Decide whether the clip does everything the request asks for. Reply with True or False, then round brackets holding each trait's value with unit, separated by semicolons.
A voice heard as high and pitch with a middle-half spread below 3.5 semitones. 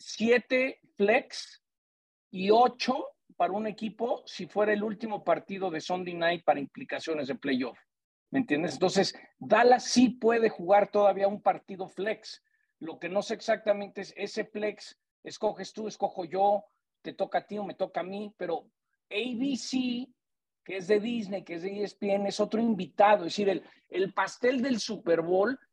True (205 Hz; 2.8 semitones)